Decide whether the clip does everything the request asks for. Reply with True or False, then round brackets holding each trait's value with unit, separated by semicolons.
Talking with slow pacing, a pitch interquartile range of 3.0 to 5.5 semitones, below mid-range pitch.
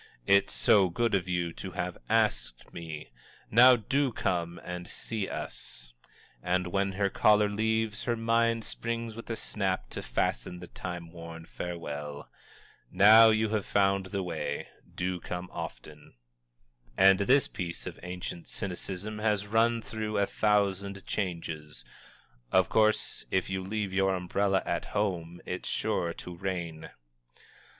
False (145 wpm; 3.4 semitones; 95 Hz)